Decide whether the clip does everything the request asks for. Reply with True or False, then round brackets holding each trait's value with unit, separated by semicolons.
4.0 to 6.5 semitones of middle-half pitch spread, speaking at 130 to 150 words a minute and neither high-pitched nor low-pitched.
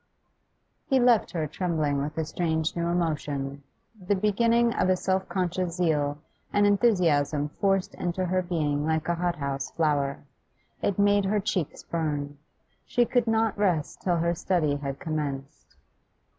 True (4.7 semitones; 145 wpm; 170 Hz)